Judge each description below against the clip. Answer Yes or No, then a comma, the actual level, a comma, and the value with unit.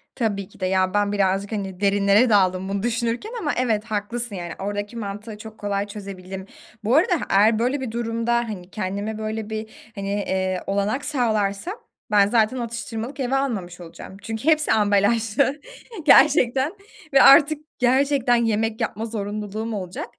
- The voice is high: Yes, high, 215 Hz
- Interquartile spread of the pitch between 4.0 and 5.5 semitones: No, average, 3.1 semitones